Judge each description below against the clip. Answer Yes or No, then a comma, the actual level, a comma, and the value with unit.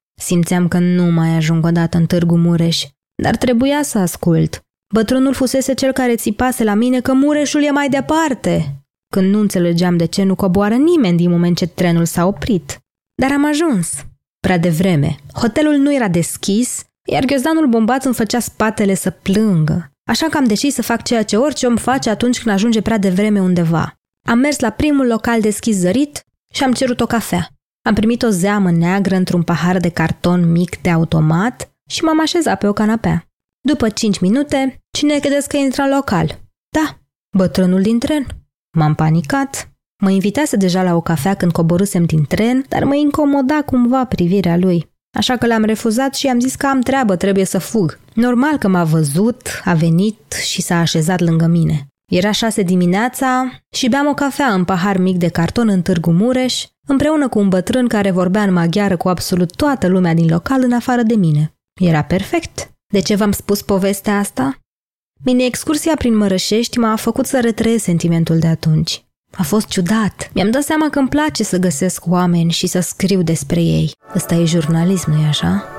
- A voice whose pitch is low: No, high, 200 Hz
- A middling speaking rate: No, fast, 185 wpm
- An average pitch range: No, wide, 6.4 semitones